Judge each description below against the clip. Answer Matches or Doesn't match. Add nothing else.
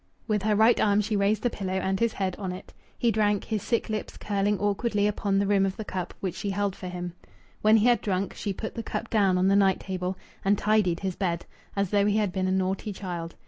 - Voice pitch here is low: Doesn't match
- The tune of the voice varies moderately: Doesn't match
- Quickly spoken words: Matches